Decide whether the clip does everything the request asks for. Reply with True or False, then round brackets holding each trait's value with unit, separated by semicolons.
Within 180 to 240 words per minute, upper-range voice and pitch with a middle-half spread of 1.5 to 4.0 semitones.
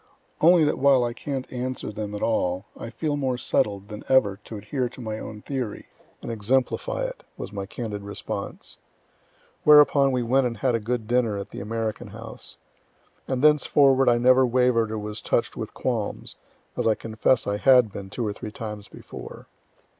False (185 wpm; 120 Hz; 3.7 semitones)